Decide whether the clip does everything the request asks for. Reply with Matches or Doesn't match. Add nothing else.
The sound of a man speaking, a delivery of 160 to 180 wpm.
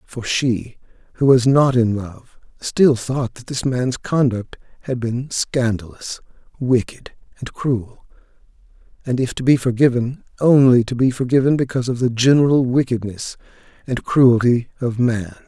Doesn't match